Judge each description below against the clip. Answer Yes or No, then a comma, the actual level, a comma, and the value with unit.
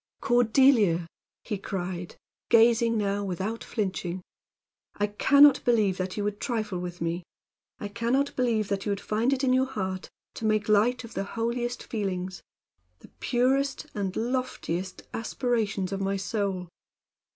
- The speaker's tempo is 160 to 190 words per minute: No, average, 150 wpm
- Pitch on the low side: No, high, 210 Hz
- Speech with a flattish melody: No, average, 4.0 semitones